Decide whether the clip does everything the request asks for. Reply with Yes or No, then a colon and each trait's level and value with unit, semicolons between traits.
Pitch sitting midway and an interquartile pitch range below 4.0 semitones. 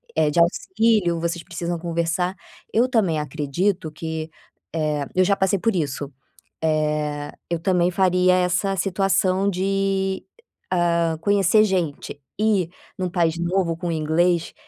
Yes: medium, 175 Hz; average, 2.9 semitones